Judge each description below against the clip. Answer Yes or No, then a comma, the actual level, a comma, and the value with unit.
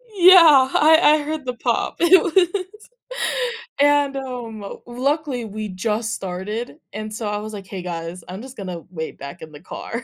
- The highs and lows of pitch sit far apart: Yes, wide, 7.1 semitones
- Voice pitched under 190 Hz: No, high, 230 Hz